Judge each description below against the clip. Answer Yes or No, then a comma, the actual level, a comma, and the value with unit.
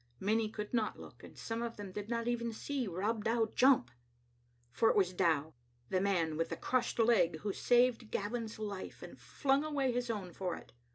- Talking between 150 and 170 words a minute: No, average, 195 wpm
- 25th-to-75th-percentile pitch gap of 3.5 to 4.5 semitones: Yes, average, 3.9 semitones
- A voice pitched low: No, high, 220 Hz